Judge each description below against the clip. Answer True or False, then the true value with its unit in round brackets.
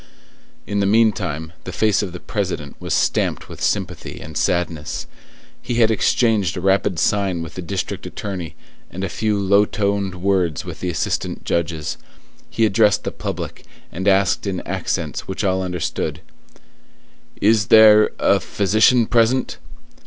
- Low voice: True (100 Hz)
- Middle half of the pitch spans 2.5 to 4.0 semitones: True (3.2 semitones)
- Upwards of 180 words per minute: False (150 wpm)